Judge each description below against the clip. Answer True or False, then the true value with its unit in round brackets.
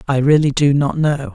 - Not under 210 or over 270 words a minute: True (225 wpm)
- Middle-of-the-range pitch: True (145 Hz)